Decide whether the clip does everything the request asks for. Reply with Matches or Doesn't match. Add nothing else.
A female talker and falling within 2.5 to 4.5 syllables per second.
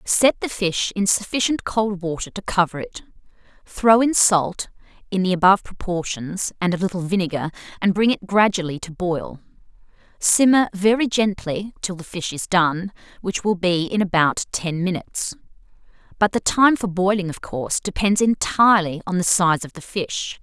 Doesn't match